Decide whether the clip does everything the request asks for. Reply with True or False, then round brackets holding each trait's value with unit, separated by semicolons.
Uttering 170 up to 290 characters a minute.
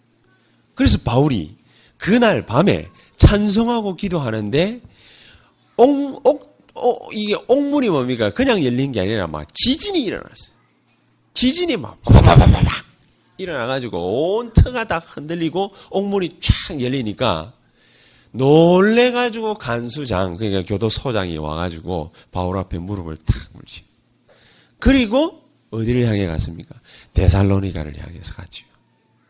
True (270 characters per minute)